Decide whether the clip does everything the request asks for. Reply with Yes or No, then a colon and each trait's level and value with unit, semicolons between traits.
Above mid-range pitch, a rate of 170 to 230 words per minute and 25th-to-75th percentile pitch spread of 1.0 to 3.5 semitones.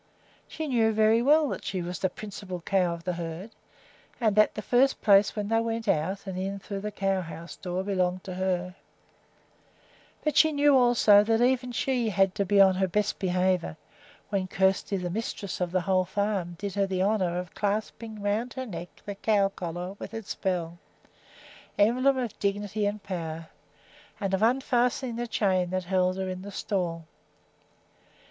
Yes: high, 195 Hz; average, 180 wpm; average, 3.2 semitones